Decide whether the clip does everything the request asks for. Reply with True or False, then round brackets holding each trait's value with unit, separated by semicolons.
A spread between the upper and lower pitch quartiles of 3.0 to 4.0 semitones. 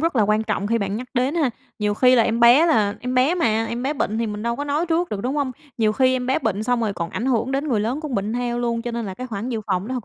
True (3.3 semitones)